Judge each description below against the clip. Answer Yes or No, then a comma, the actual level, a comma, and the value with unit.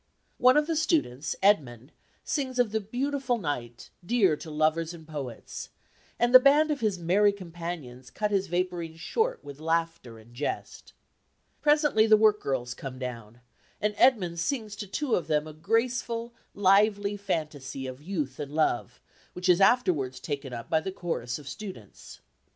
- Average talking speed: Yes, average, 160 wpm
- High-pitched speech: No, medium, 175 Hz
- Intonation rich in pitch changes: Yes, wide, 7.4 semitones